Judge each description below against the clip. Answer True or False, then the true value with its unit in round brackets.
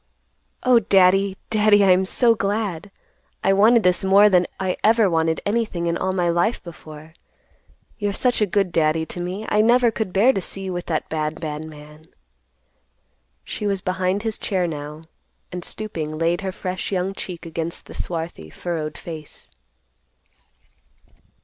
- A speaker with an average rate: True (160 wpm)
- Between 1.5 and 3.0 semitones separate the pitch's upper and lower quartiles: False (3.8 semitones)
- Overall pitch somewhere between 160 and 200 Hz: True (185 Hz)